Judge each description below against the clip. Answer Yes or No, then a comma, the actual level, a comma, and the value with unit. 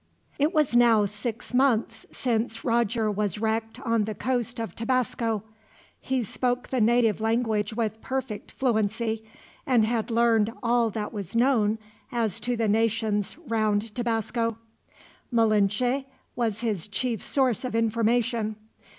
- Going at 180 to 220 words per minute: No, slow, 135 wpm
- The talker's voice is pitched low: No, high, 230 Hz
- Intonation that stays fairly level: Yes, narrow, 2.0 semitones